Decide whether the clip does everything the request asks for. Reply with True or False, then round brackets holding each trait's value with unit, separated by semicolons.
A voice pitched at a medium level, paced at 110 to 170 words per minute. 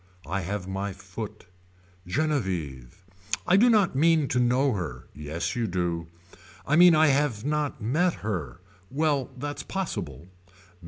False (120 Hz; 140 wpm)